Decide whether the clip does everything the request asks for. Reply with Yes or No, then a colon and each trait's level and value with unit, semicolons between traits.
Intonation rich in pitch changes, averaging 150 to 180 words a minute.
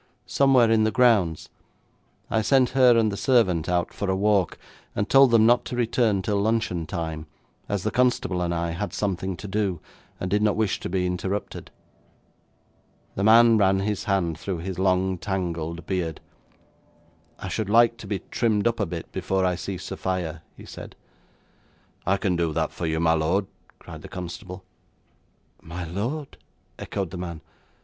No: average, 3.8 semitones; average, 170 wpm